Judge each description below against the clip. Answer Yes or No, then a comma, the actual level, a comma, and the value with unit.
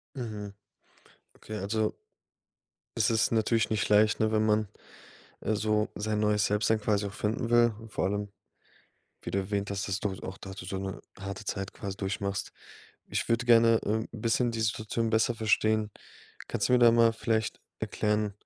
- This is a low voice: Yes, low, 105 Hz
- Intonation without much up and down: Yes, narrow, 1.6 semitones